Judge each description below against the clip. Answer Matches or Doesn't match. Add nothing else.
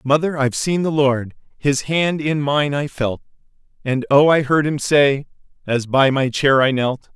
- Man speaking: Matches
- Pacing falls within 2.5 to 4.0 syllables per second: Doesn't match